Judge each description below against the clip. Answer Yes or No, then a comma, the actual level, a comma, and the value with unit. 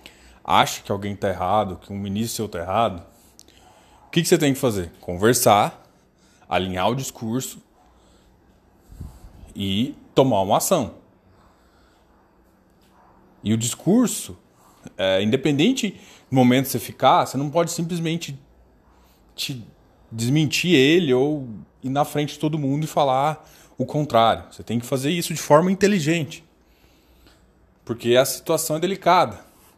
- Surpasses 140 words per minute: No, average, 135 wpm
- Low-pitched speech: Yes, low, 120 Hz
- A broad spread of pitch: Yes, wide, 8.5 semitones